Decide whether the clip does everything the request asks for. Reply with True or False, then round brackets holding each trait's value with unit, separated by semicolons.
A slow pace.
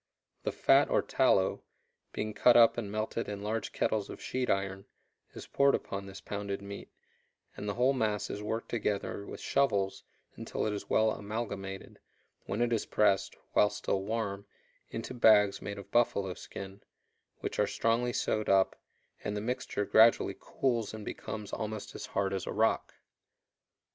False (165 wpm)